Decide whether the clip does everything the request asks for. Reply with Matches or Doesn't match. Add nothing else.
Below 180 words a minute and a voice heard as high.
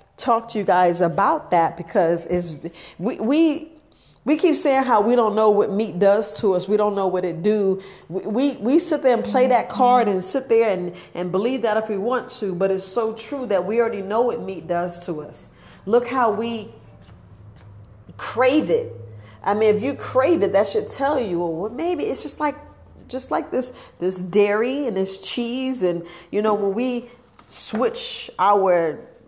Doesn't match